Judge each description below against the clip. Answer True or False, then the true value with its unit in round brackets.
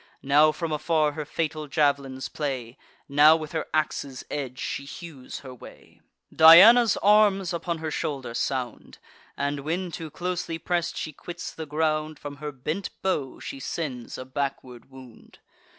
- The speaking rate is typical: True (150 wpm)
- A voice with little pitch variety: False (3.3 semitones)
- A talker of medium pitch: True (150 Hz)